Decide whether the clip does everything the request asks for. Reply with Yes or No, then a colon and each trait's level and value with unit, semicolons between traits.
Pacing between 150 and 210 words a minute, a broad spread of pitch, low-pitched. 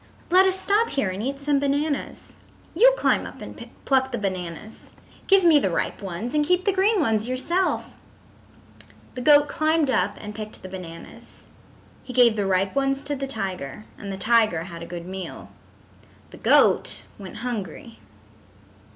No: average, 170 wpm; wide, 7.3 semitones; high, 245 Hz